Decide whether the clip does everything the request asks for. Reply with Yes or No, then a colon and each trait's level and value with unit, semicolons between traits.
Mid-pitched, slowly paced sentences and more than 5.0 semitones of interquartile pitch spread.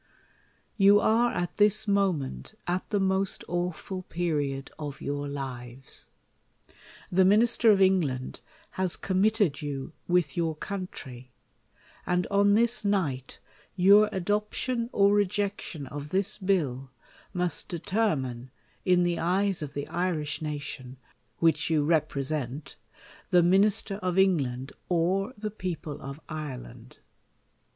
Yes: medium, 175 Hz; slow, 125 wpm; wide, 5.6 semitones